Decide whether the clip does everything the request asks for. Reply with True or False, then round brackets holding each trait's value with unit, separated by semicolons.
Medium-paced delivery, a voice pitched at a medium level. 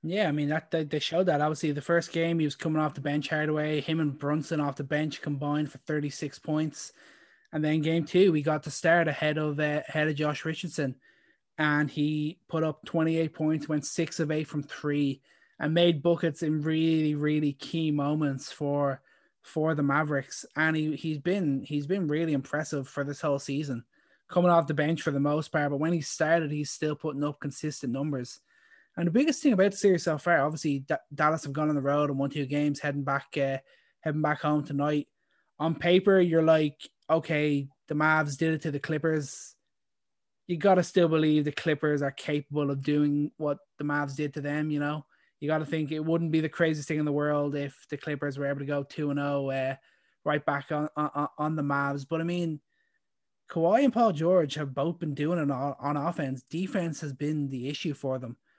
False (210 wpm; 150 Hz)